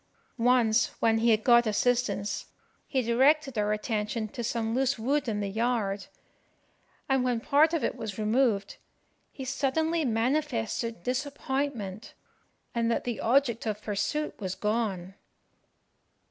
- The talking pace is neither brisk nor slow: No, slow, 130 wpm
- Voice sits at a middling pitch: No, high, 235 Hz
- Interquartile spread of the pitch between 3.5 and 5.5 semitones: Yes, average, 3.8 semitones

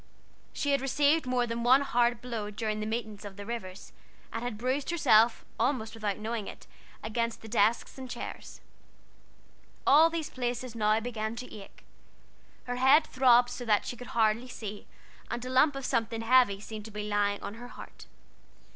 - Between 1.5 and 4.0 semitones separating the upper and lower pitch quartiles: Yes, average, 2.8 semitones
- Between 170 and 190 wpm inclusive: Yes, average, 180 wpm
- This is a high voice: Yes, high, 235 Hz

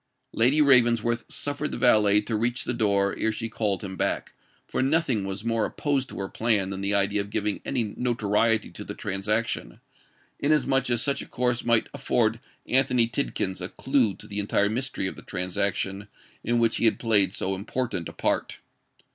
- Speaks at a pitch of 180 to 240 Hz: No, low, 110 Hz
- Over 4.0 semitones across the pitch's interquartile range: No, average, 3.5 semitones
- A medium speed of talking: Yes, average, 185 wpm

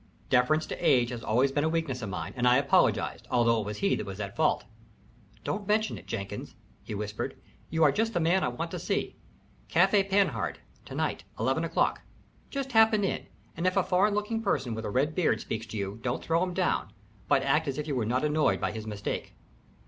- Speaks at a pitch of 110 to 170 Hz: Yes, medium, 140 Hz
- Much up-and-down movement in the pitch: Yes, wide, 8.6 semitones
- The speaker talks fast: Yes, fast, 220 wpm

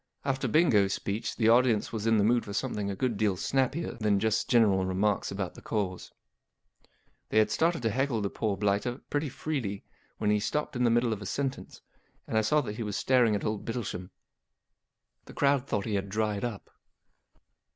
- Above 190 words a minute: Yes, fast, 205 wpm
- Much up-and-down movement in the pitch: No, average, 3.5 semitones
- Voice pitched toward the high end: No, low, 110 Hz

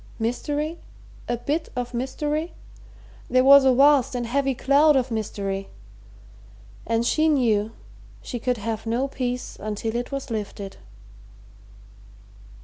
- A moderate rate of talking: No, slow, 125 wpm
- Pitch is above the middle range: Yes, very high, 250 Hz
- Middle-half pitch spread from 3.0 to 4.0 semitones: Yes, average, 3.6 semitones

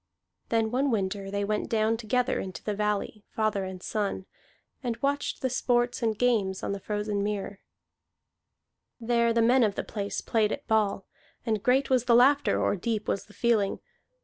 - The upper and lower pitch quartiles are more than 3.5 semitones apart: No, average, 2.9 semitones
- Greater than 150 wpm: Yes, average, 175 wpm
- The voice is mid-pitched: No, high, 220 Hz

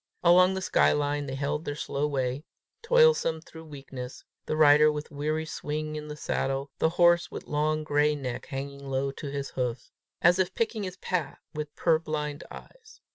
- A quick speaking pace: No, average, 180 wpm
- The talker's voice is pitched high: No, medium, 150 Hz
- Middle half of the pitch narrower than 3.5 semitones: Yes, average, 2.7 semitones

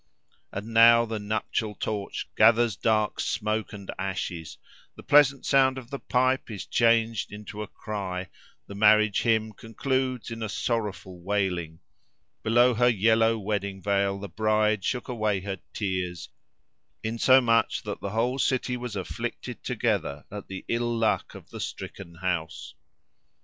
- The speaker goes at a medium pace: Yes, average, 145 wpm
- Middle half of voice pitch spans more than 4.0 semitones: No, average, 2.9 semitones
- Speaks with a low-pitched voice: Yes, low, 110 Hz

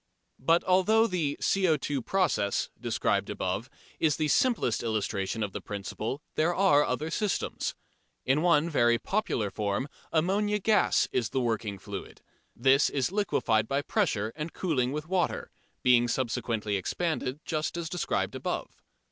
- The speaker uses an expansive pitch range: Yes, wide, 7.3 semitones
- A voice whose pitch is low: No, medium, 145 Hz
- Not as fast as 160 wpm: Yes, average, 140 wpm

